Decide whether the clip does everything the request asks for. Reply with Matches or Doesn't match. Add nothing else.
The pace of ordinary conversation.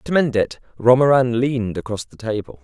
Matches